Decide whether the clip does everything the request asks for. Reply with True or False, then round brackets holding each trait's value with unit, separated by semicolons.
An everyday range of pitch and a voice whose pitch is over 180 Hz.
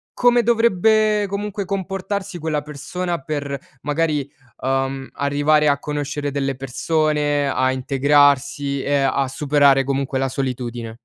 False (4.0 semitones; 145 Hz)